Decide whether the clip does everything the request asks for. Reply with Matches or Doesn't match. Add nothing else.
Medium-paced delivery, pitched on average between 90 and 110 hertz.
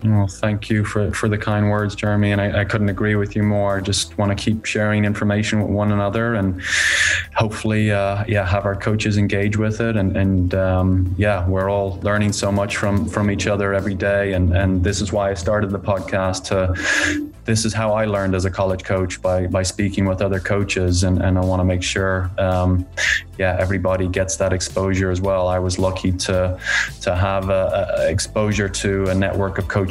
Doesn't match